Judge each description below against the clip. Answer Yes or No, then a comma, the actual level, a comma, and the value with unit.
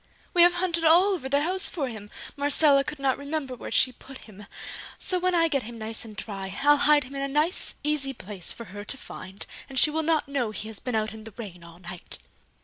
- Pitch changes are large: Yes, wide, 5.8 semitones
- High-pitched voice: Yes, very high, 270 Hz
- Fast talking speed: Yes, fast, 240 wpm